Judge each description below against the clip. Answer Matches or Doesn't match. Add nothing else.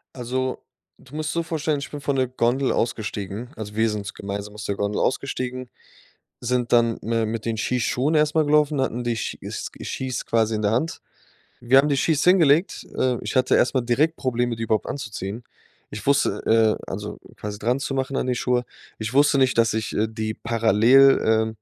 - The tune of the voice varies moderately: Matches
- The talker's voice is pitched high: Doesn't match